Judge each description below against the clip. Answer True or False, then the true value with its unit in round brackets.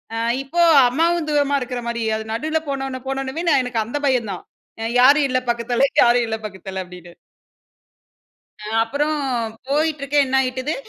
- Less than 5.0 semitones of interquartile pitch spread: True (3.8 semitones)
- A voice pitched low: False (260 Hz)